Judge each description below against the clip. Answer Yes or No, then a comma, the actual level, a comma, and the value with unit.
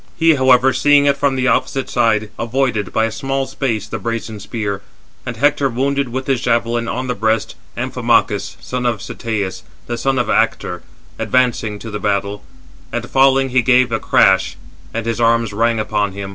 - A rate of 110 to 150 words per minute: No, average, 180 wpm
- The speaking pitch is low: Yes, low, 115 Hz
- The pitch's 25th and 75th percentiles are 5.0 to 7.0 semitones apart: No, average, 3.2 semitones